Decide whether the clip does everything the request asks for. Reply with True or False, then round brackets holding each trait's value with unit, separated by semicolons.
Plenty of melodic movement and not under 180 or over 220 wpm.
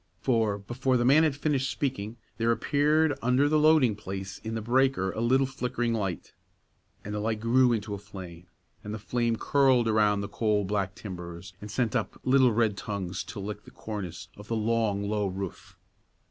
False (4.0 semitones; 190 wpm)